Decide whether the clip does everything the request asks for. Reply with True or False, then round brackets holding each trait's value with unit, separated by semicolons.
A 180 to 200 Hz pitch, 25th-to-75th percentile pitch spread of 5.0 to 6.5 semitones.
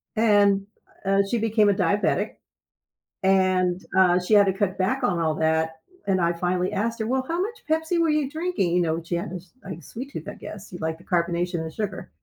False (190 Hz; 4.1 semitones)